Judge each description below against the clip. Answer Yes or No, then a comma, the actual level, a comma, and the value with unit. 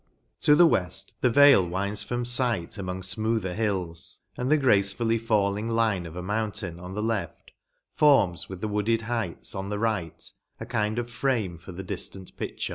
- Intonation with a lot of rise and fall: No, average, 3.6 semitones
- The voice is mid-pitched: No, low, 105 Hz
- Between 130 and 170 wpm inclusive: No, average, 180 wpm